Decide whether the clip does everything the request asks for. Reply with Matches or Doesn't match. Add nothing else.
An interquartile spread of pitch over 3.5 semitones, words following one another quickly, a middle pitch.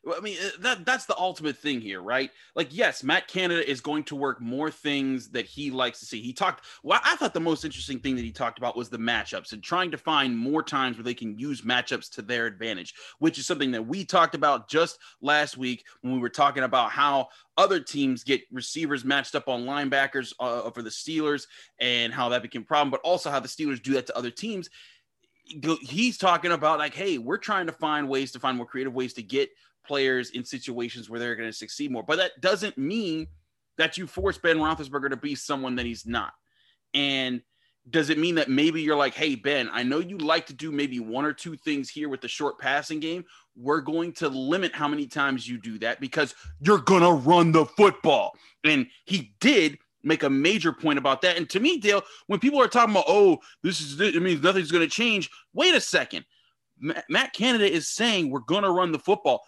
Matches